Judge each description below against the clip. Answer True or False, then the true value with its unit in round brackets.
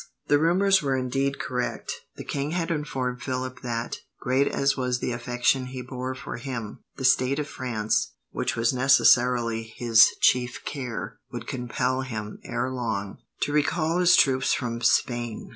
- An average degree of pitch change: False (2.3 semitones)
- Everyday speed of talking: True (160 wpm)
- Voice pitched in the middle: False (125 Hz)